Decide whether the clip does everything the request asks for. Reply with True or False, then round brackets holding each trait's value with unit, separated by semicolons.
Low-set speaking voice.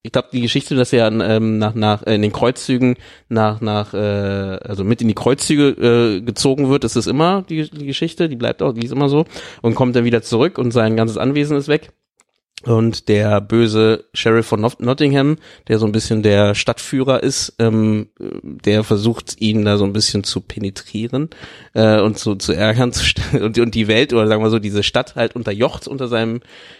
True (115 Hz)